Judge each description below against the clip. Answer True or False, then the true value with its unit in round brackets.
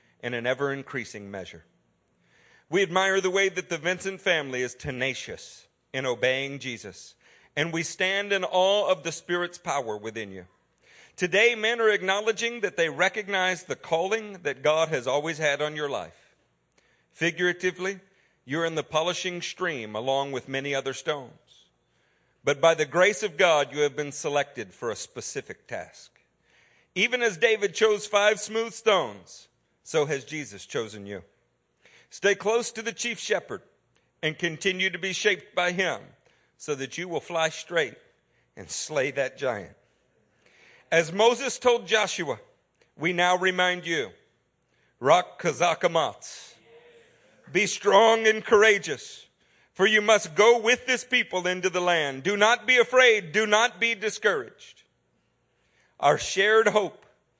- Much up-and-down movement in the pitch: True (6.3 semitones)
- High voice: False (180 Hz)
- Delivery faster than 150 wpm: False (145 wpm)